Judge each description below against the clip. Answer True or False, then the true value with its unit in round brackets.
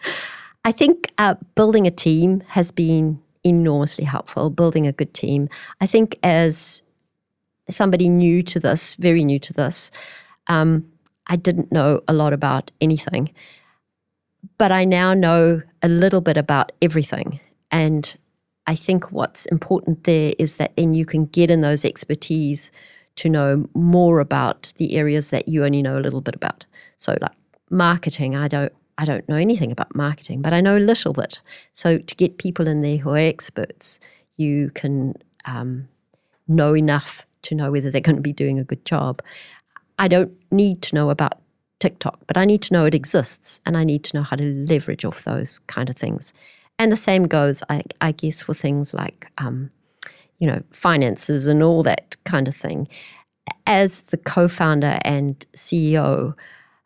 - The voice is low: False (160 Hz)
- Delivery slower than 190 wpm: True (175 wpm)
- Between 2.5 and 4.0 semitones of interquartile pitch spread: True (3.1 semitones)